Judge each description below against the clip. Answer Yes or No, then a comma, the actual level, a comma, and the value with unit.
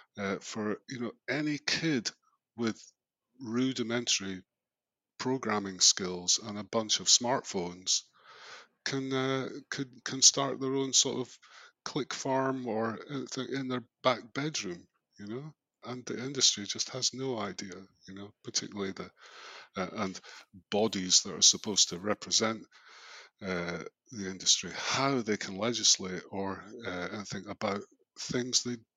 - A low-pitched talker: Yes, low, 120 Hz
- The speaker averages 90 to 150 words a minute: Yes, average, 140 wpm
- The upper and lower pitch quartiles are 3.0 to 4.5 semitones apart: No, average, 5.2 semitones